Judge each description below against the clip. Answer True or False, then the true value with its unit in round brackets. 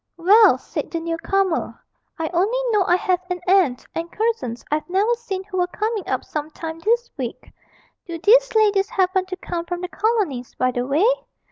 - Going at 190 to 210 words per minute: True (195 wpm)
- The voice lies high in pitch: True (370 Hz)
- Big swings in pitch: False (4.2 semitones)